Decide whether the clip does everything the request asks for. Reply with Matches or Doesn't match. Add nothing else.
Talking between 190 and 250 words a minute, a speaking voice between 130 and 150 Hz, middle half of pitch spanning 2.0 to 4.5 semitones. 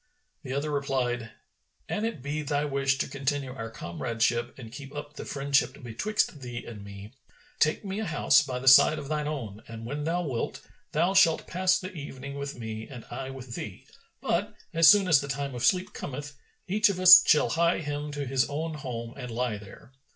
Matches